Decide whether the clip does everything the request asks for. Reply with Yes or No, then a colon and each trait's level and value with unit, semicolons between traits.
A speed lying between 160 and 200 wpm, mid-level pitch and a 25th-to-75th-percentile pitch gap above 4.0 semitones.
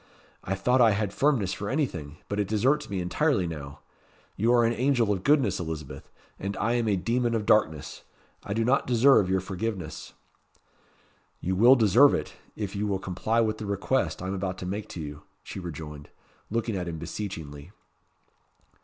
No: average, 180 wpm; low, 100 Hz; average, 4.4 semitones